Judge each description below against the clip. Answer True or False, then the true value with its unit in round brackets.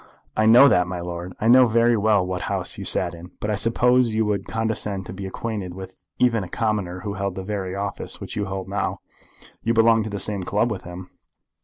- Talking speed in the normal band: False (225 wpm)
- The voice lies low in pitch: True (100 Hz)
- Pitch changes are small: False (3.1 semitones)